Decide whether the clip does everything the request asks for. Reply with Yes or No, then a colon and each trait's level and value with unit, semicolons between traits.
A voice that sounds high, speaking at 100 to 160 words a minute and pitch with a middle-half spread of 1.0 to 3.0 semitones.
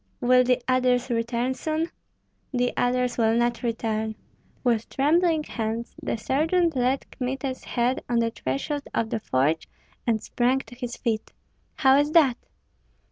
Yes: high, 245 Hz; average, 145 wpm; narrow, 2.6 semitones